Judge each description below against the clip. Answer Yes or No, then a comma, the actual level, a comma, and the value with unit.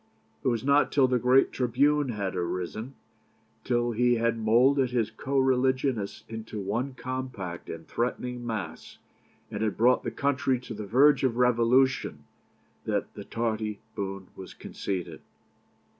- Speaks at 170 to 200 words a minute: No, average, 145 wpm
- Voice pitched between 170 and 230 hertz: No, low, 120 Hz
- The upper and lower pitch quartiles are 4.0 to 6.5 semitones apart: No, average, 3.1 semitones